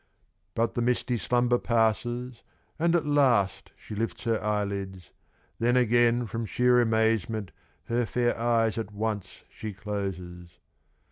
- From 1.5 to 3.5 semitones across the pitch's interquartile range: Yes, average, 2.7 semitones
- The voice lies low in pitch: Yes, low, 115 Hz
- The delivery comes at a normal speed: No, slow, 130 wpm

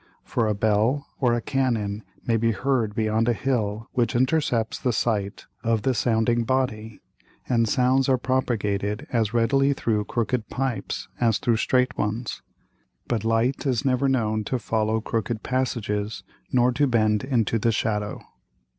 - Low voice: Yes, low, 115 Hz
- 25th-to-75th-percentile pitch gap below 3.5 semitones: Yes, average, 2.9 semitones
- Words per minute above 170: No, average, 155 wpm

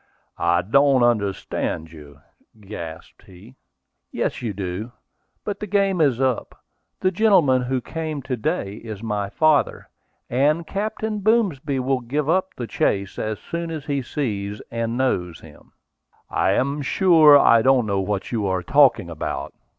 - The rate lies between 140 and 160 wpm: Yes, average, 150 wpm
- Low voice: Yes, low, 125 Hz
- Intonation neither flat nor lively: No, wide, 7.1 semitones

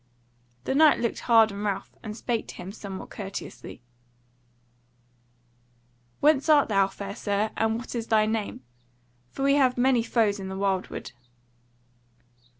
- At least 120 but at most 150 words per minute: Yes, average, 145 wpm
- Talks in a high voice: Yes, high, 220 Hz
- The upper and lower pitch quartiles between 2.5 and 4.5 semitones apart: Yes, average, 3.5 semitones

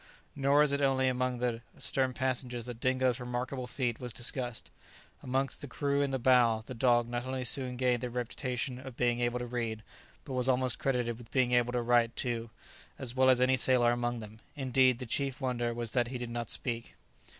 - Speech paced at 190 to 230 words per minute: Yes, fast, 205 wpm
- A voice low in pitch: Yes, low, 125 Hz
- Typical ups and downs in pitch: No, narrow, 1.4 semitones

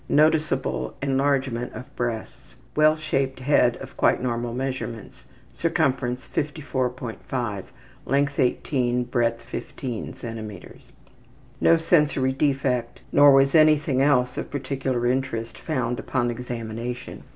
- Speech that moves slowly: Yes, slow, 105 wpm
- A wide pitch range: No, average, 2.7 semitones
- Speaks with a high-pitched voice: No, low, 130 Hz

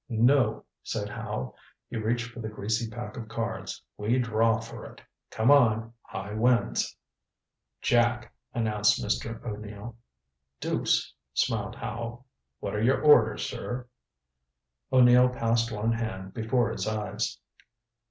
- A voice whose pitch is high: No, low, 115 Hz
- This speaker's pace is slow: Yes, slow, 125 wpm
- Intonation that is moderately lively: No, narrow, 1.8 semitones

